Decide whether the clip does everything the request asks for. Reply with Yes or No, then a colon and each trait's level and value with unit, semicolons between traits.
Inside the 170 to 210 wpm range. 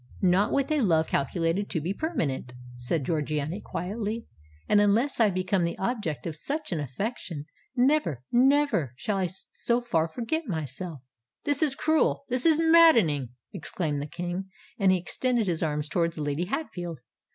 No: average, 150 wpm